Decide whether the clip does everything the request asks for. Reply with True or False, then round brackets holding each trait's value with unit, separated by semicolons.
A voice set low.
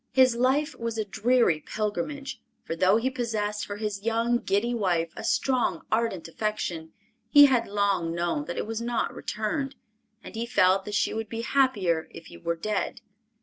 False (220 Hz)